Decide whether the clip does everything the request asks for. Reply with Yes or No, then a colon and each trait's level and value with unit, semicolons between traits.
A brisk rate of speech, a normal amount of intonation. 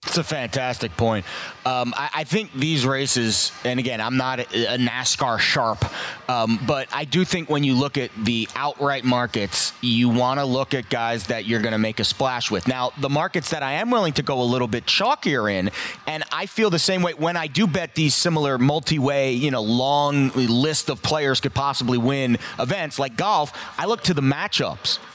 Yes: fast, 210 wpm; average, 3.9 semitones